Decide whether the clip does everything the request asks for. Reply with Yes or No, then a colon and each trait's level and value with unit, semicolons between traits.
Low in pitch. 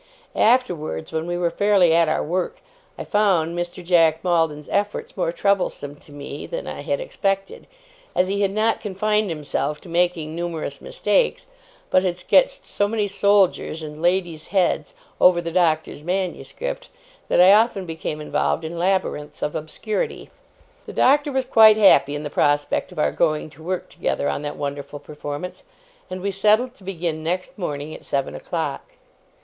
No: medium, 180 Hz